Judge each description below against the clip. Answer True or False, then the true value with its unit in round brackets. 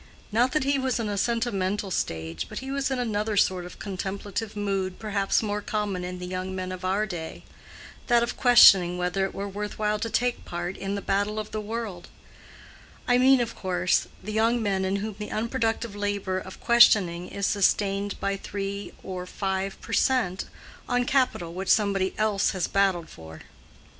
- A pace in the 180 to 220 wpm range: True (185 wpm)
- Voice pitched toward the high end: True (200 Hz)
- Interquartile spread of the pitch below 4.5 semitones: True (2.9 semitones)